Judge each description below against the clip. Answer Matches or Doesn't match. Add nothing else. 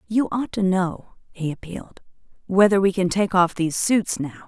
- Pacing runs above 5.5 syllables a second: Doesn't match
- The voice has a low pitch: Doesn't match